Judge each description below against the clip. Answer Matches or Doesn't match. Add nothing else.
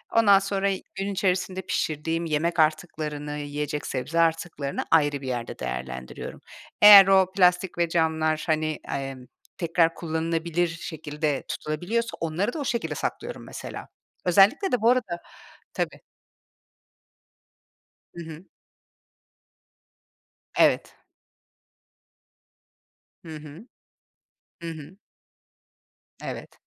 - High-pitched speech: Doesn't match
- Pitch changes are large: Doesn't match